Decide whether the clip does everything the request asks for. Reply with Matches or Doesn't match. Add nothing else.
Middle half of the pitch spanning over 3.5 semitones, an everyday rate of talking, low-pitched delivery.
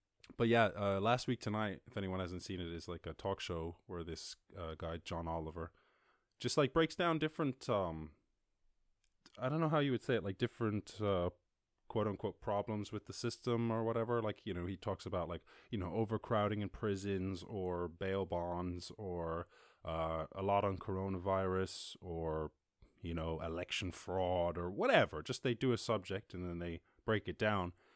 Matches